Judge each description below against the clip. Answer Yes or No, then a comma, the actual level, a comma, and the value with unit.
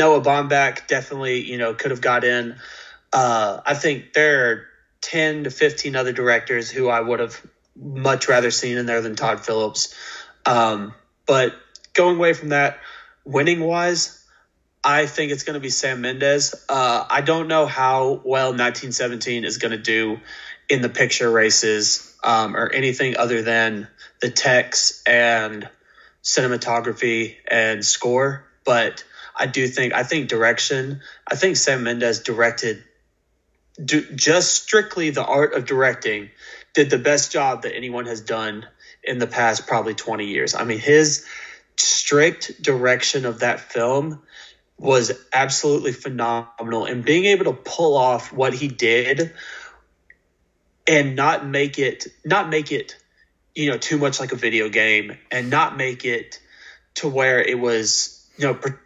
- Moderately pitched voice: No, low, 125 Hz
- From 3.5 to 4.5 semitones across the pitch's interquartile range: Yes, average, 3.8 semitones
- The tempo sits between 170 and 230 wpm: No, average, 155 wpm